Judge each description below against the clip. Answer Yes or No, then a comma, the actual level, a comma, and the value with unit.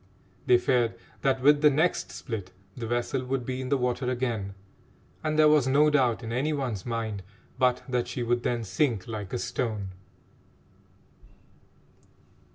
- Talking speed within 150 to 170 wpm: Yes, average, 160 wpm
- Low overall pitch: Yes, low, 125 Hz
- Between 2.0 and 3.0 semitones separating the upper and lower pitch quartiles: Yes, narrow, 2.6 semitones